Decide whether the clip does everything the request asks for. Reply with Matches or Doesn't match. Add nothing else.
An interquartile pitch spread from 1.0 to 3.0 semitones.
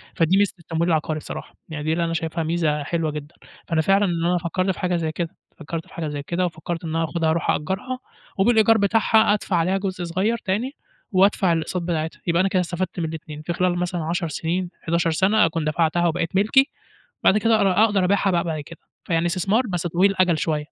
Matches